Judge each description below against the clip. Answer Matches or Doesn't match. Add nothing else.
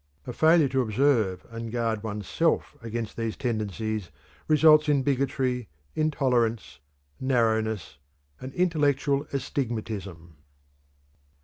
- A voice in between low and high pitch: Doesn't match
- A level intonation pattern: Doesn't match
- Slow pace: Matches